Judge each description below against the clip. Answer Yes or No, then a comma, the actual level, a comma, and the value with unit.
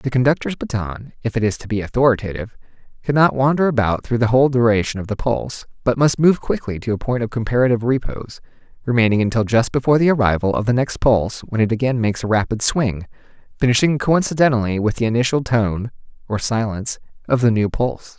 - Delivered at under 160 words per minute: No, average, 190 wpm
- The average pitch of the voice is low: Yes, low, 120 Hz